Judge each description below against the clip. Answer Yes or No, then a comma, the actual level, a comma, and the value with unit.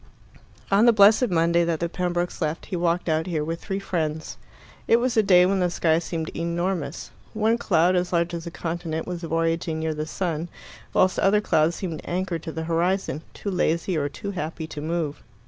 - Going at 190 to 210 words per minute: Yes, average, 200 wpm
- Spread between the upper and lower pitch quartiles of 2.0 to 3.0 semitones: Yes, narrow, 2.4 semitones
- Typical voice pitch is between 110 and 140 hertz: No, medium, 170 Hz